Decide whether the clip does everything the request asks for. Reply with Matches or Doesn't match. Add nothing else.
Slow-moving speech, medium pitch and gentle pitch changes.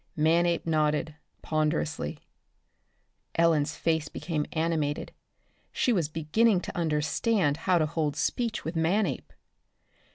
Matches